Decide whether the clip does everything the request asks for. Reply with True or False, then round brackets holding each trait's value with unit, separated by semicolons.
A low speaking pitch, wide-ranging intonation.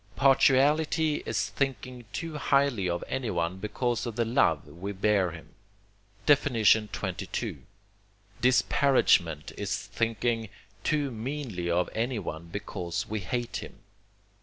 True (115 Hz; 6.4 semitones)